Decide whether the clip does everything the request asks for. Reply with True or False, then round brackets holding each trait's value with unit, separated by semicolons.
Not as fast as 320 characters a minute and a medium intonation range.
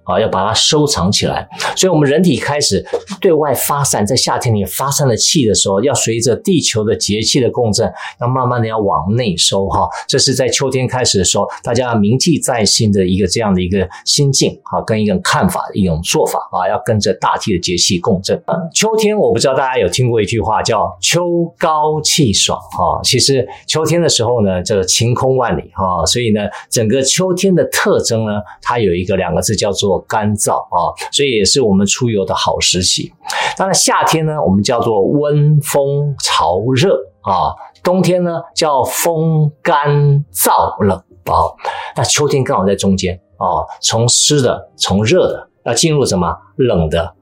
False (270 characters per minute; 7.0 semitones)